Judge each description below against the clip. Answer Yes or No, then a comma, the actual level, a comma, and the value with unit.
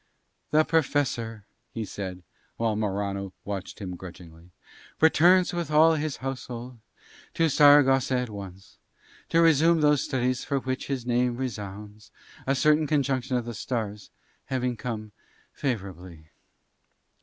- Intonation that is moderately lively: No, wide, 5.8 semitones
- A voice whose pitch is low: Yes, low, 125 Hz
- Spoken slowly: Yes, slow, 125 wpm